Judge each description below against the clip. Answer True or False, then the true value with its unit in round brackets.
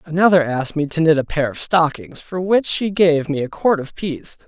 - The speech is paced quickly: True (240 wpm)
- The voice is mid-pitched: True (160 Hz)